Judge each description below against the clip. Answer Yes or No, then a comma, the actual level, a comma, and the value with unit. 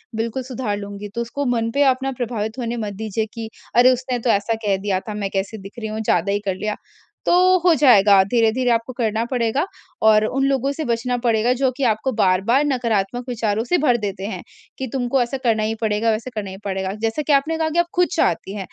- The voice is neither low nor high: No, high, 230 Hz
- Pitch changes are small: No, average, 3.5 semitones